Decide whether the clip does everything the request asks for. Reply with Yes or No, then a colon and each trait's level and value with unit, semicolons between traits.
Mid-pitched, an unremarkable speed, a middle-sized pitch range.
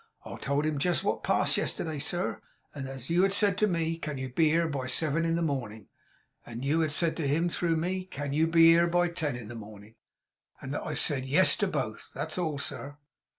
No: medium, 155 Hz; fast, 240 wpm; average, 3.7 semitones